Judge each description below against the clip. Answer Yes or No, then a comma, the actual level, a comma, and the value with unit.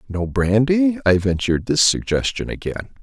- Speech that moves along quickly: No, average, 140 wpm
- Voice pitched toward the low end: Yes, low, 115 Hz